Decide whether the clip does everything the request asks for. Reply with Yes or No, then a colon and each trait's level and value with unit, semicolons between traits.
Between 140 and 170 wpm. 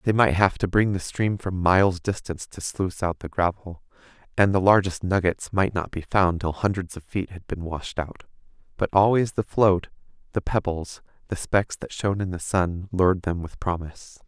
No: average, 200 wpm